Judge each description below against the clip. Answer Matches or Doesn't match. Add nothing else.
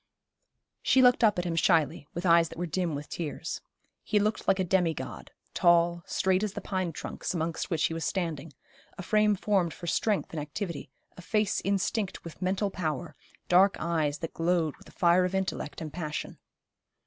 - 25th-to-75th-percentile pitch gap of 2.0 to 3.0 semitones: Matches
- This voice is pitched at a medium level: Matches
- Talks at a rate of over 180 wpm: Matches